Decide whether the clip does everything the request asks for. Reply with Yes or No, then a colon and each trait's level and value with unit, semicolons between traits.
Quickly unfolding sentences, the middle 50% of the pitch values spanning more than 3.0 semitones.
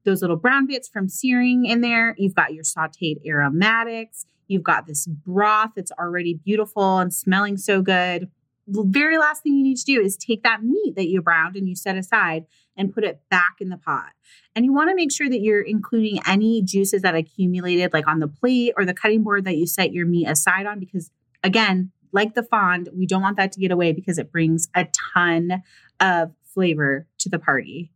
Yes: fast, 210 wpm; average, 4.0 semitones